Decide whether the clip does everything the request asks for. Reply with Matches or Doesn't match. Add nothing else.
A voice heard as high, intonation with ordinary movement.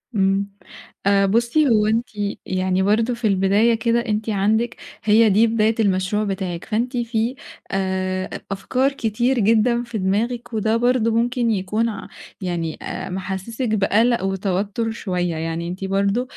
Matches